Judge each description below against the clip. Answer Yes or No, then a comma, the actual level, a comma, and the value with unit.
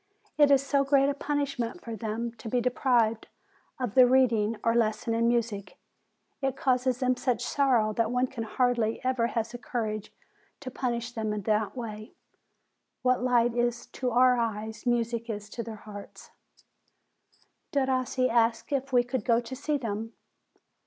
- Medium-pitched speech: No, high, 240 Hz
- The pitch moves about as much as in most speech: No, narrow, 2.3 semitones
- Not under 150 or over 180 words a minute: Yes, average, 165 wpm